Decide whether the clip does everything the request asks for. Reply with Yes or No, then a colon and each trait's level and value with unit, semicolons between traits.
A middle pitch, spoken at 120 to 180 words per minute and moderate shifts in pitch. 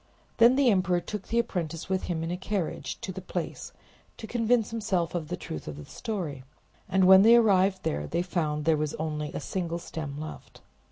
No: medium, 180 Hz; fast, 205 wpm; average, 4.6 semitones